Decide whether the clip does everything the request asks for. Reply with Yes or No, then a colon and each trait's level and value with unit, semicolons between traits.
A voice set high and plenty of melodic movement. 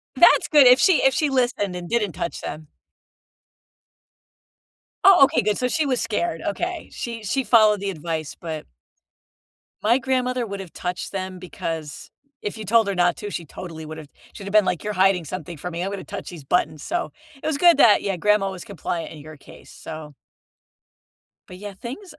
Yes: high, 195 Hz; wide, 5.7 semitones